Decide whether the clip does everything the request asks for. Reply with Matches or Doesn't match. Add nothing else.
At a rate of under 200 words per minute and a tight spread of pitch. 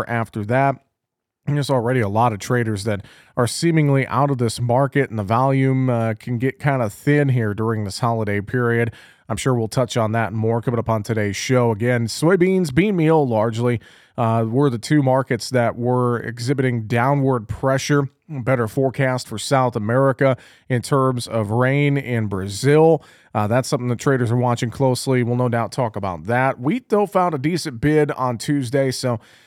Doesn't match